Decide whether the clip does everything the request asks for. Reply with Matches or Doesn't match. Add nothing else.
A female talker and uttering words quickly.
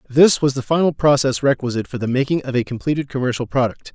Doesn't match